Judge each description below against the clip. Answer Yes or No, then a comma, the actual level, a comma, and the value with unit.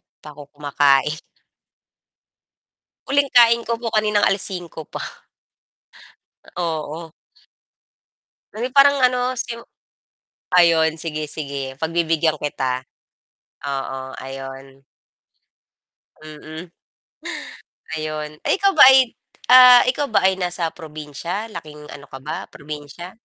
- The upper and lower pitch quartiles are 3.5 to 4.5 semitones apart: No, average, 5.2 semitones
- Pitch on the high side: No, medium, 160 Hz